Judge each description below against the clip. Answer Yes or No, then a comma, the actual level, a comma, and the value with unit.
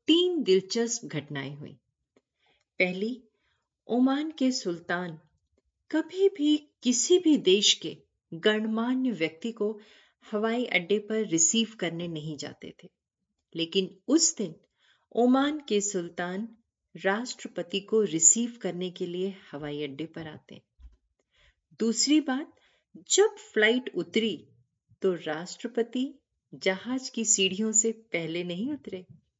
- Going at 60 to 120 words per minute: Yes, slow, 110 wpm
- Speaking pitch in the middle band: No, high, 210 Hz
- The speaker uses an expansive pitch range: Yes, wide, 5.9 semitones